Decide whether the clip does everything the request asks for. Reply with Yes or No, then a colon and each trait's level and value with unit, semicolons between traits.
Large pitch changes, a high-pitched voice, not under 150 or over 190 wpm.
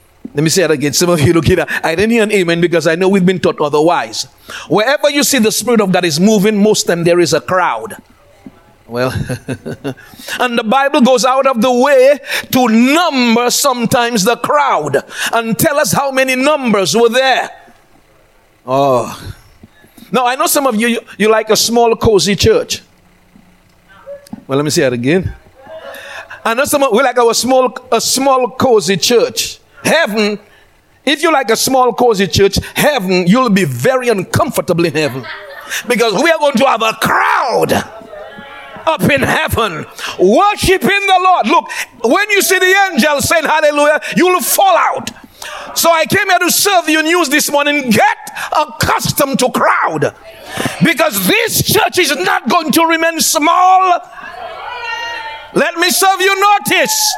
Yes: wide, 7.4 semitones; very high, 250 Hz; average, 170 wpm